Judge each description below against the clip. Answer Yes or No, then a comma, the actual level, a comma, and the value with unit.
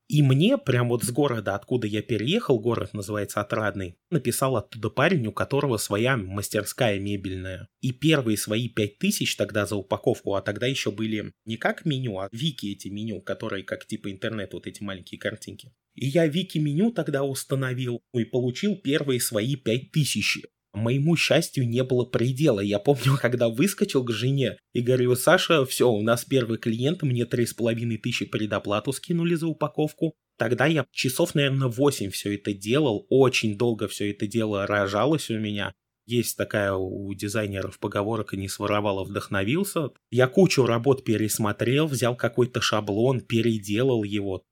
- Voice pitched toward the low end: Yes, low, 120 Hz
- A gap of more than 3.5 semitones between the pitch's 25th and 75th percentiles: Yes, average, 4.6 semitones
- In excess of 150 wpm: Yes, fast, 160 wpm